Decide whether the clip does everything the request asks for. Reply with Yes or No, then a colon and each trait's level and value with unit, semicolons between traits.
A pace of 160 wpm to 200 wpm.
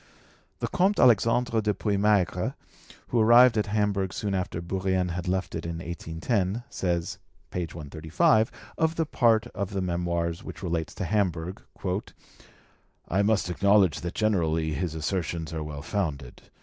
No: average, 145 wpm